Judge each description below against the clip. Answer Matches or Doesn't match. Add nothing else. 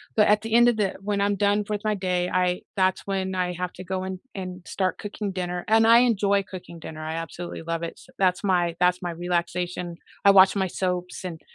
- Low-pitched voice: Doesn't match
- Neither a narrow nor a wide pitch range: Doesn't match